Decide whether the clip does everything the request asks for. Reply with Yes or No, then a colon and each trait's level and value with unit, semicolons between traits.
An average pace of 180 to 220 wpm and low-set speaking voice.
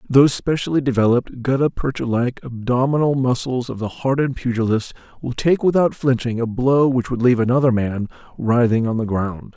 No: average, 170 wpm; low, 125 Hz